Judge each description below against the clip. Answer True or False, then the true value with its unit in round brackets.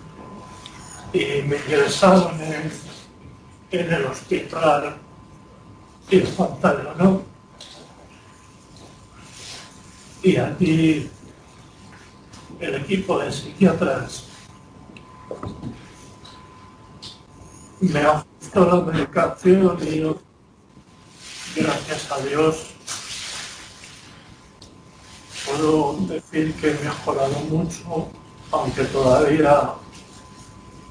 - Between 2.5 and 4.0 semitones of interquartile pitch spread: True (2.9 semitones)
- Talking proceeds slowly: True (65 wpm)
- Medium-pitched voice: True (155 Hz)